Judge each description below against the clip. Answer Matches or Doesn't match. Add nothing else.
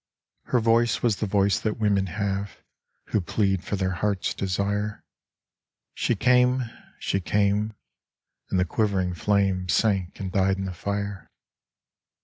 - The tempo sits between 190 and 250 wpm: Doesn't match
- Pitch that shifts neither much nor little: Doesn't match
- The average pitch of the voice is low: Matches